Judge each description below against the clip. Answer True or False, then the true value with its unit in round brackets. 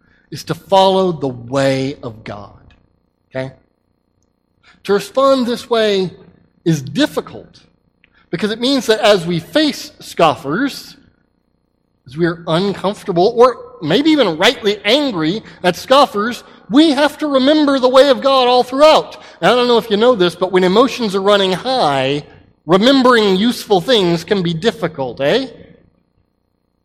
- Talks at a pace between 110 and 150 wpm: True (145 wpm)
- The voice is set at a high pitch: True (195 Hz)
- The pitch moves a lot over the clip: True (8.2 semitones)